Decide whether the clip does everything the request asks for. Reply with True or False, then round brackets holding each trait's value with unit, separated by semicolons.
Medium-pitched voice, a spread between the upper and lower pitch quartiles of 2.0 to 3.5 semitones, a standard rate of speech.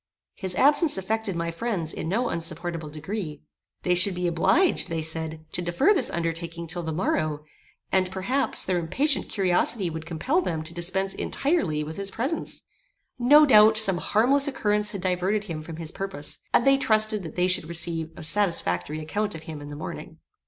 False (180 Hz; 4.8 semitones; 180 wpm)